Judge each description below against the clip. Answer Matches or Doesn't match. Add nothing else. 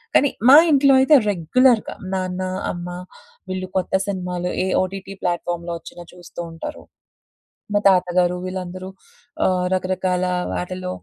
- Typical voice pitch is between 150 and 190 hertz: Matches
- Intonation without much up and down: Matches